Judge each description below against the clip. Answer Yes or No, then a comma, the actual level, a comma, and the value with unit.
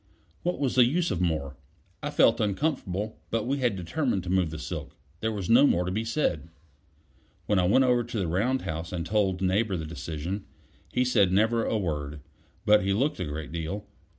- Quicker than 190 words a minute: Yes, fast, 205 wpm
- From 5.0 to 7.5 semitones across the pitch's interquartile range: Yes, wide, 5.5 semitones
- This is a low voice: Yes, low, 100 Hz